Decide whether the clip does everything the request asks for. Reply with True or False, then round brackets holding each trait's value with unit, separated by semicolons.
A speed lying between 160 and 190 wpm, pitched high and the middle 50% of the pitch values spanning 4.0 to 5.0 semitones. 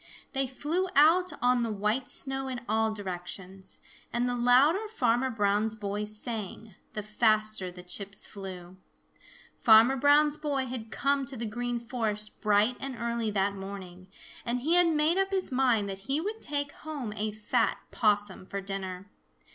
True (165 wpm; 225 Hz; 4.7 semitones)